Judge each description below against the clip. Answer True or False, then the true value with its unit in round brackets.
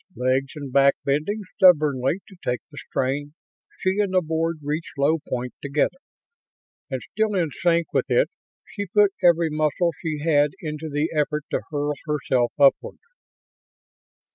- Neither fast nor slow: True (150 wpm)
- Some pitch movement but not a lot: True (3.4 semitones)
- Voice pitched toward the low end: False (150 Hz)